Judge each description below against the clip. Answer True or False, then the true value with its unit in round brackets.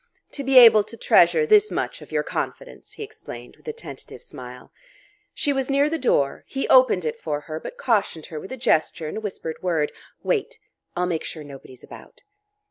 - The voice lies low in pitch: False (230 Hz)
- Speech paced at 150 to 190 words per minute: False (200 wpm)